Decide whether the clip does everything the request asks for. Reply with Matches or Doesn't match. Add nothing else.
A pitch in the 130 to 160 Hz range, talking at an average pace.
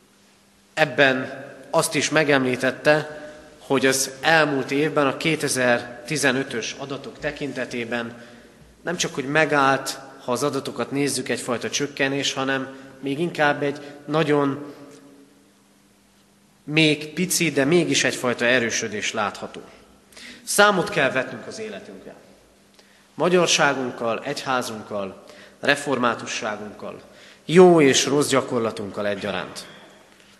Doesn't match